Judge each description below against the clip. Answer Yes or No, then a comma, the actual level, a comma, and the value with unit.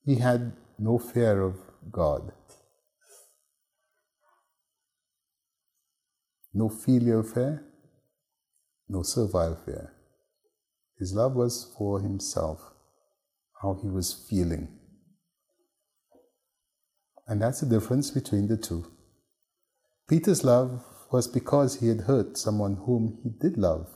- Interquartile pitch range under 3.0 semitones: No, average, 4.8 semitones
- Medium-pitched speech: No, low, 120 Hz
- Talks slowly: Yes, slow, 100 wpm